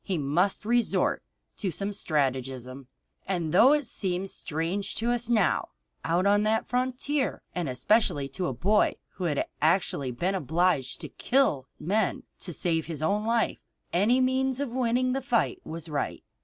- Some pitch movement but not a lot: No, wide, 7.0 semitones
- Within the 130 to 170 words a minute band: Yes, average, 160 wpm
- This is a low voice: No, high, 190 Hz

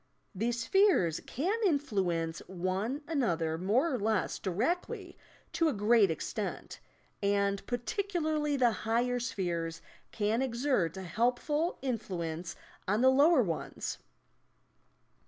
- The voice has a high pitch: Yes, high, 230 Hz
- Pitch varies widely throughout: Yes, wide, 7.1 semitones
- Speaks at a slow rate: Yes, slow, 115 wpm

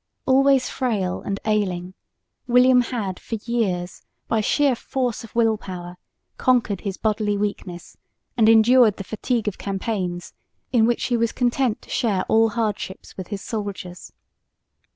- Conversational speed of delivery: Yes, average, 145 wpm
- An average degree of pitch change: Yes, average, 3.6 semitones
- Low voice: No, high, 220 Hz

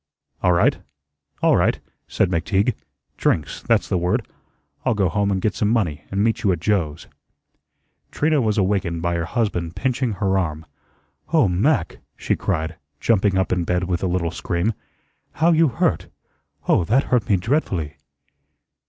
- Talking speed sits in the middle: Yes, average, 160 wpm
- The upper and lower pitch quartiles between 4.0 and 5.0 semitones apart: Yes, average, 4.6 semitones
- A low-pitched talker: Yes, very low, 95 Hz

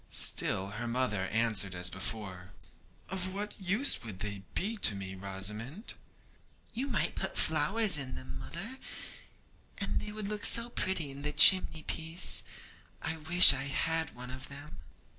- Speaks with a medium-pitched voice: Yes, medium, 145 Hz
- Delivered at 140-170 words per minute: Yes, average, 155 wpm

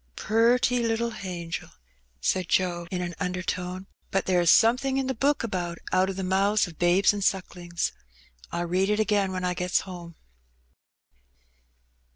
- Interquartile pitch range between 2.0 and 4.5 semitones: Yes, average, 3.2 semitones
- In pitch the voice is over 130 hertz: Yes, high, 190 Hz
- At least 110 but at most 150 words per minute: No, average, 160 wpm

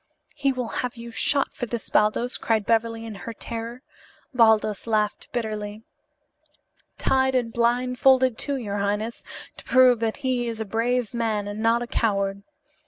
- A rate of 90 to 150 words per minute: No, average, 160 wpm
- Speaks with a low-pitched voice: No, high, 230 Hz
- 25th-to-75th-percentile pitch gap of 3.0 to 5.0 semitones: No, narrow, 2.4 semitones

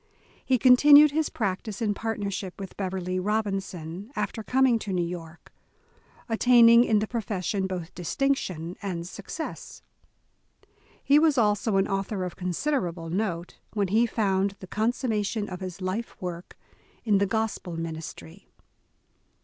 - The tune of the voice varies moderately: Yes, average, 3.7 semitones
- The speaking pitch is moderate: No, high, 200 Hz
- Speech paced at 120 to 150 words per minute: Yes, slow, 135 wpm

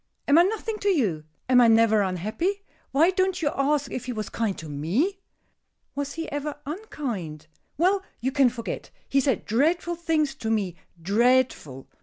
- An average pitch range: No, wide, 7.2 semitones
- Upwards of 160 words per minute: Yes, average, 170 wpm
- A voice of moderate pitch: No, very high, 270 Hz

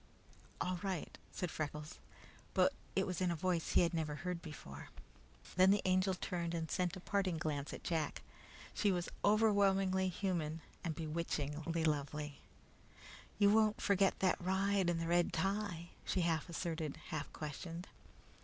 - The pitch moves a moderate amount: Yes, average, 3.1 semitones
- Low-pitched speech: No, medium, 175 Hz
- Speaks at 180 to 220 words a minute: No, average, 155 wpm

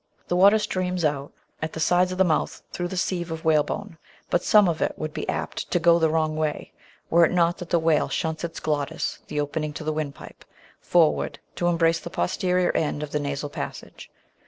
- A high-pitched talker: No, medium, 165 Hz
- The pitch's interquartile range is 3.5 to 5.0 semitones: No, narrow, 2.4 semitones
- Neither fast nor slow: No, fast, 210 wpm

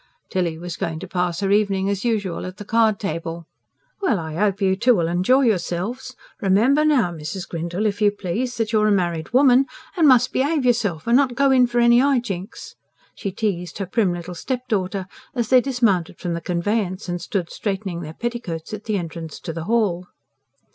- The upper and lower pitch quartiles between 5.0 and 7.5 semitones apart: Yes, wide, 5.4 semitones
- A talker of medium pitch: No, high, 200 Hz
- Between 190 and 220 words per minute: Yes, average, 195 wpm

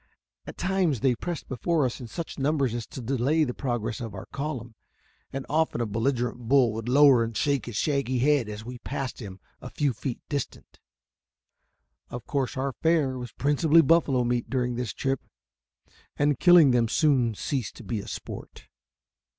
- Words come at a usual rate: Yes, average, 185 wpm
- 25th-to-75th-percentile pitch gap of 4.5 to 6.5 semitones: No, average, 3.4 semitones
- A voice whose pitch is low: Yes, low, 130 Hz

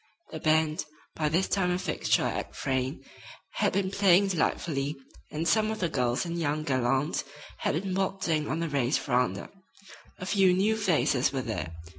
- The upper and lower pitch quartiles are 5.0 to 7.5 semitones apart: Yes, wide, 5.4 semitones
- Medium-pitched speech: Yes, medium, 160 Hz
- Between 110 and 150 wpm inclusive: No, average, 170 wpm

